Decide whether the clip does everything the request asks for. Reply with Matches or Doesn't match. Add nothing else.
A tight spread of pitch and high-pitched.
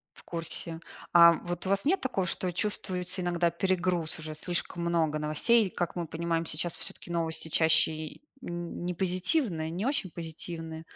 Doesn't match